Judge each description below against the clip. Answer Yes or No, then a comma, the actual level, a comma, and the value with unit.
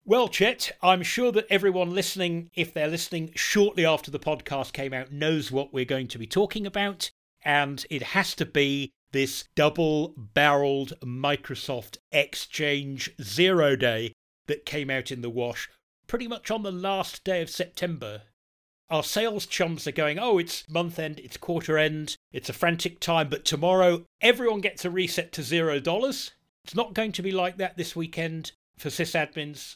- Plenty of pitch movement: No, average, 4.6 semitones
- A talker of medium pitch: Yes, medium, 160 Hz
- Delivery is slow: No, average, 175 wpm